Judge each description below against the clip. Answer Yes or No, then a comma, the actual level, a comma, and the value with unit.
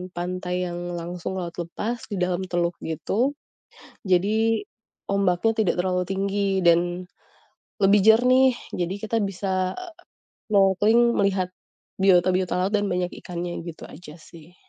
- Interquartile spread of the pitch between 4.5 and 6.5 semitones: No, average, 2.7 semitones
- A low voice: No, medium, 185 Hz